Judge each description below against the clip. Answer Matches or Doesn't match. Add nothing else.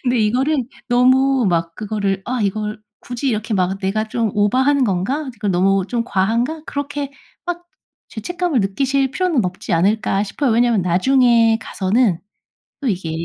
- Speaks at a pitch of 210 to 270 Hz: Matches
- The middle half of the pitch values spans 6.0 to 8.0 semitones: Doesn't match